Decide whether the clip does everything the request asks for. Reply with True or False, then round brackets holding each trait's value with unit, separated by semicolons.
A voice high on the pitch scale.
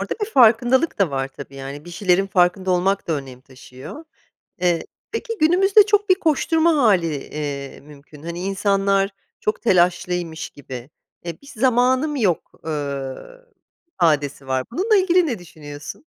False (180 Hz)